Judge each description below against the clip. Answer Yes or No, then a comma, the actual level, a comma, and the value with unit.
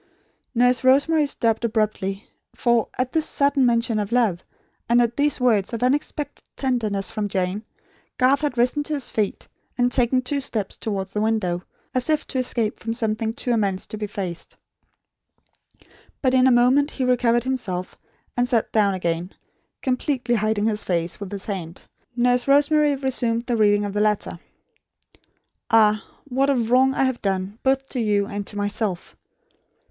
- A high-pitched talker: Yes, high, 235 Hz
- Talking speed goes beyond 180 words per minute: No, average, 165 wpm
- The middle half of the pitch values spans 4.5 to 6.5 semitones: No, average, 3.9 semitones